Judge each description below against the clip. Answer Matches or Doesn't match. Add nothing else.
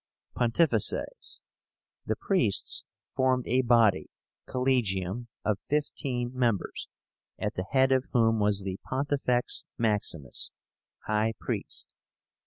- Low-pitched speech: Matches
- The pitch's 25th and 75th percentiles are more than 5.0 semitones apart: Doesn't match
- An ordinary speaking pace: Doesn't match